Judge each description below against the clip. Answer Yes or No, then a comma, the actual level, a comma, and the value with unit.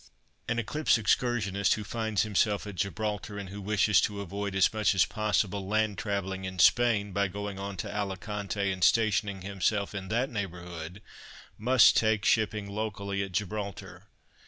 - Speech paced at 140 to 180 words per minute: Yes, average, 160 wpm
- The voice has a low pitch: Yes, low, 100 Hz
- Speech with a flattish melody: Yes, narrow, 1.7 semitones